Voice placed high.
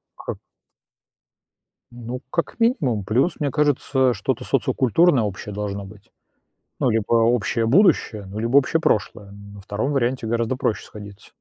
No: low, 115 Hz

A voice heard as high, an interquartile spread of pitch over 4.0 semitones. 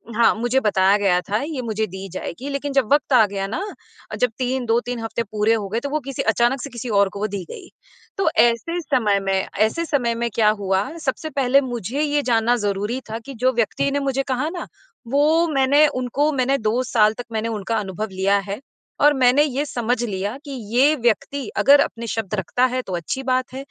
Yes: high, 240 Hz; average, 4.4 semitones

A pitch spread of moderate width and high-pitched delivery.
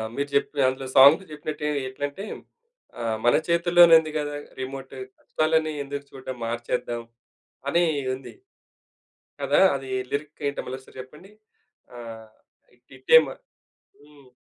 No: average, 3.0 semitones; medium, 140 Hz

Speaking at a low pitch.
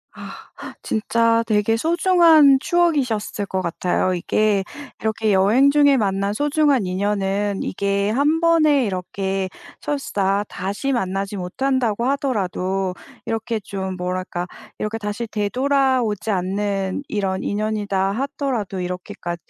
No: high, 210 Hz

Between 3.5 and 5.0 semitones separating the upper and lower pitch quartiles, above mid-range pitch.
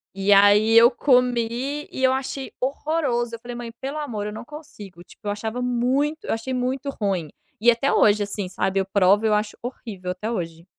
Yes: average, 4.2 semitones; high, 230 Hz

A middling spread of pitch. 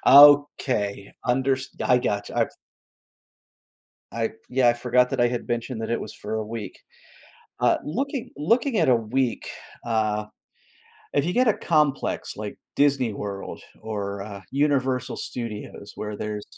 Yes: average, 4.6 semitones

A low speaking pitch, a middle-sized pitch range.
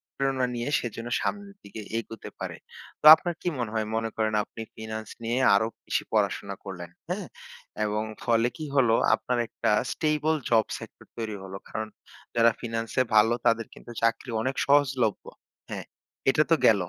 Yes: low, 115 Hz; average, 3.1 semitones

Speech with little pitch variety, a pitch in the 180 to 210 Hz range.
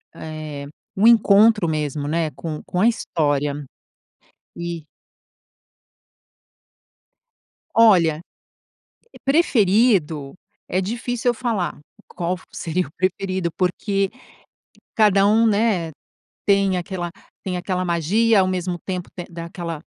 No: average, 4.0 semitones; medium, 185 Hz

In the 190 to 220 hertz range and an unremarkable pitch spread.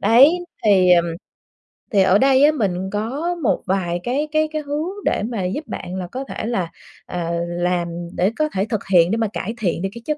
No: high, 210 Hz; wide, 7.1 semitones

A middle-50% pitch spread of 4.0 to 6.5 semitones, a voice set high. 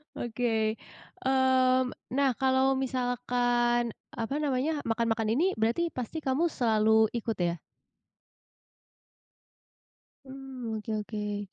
No: average, 2.9 semitones; high, 245 Hz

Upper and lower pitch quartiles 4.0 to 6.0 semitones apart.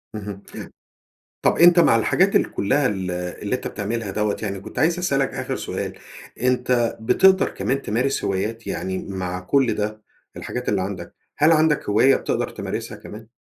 Yes: average, 5.3 semitones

